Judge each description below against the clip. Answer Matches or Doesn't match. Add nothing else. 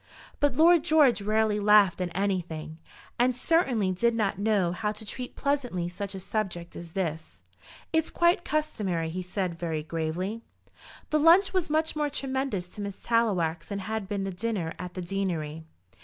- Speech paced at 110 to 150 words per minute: Doesn't match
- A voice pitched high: Matches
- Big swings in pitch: Matches